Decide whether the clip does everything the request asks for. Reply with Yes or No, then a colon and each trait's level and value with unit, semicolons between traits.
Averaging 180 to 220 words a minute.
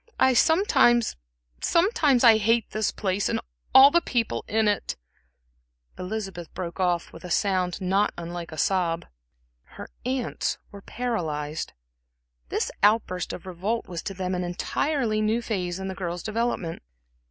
No: average, 150 wpm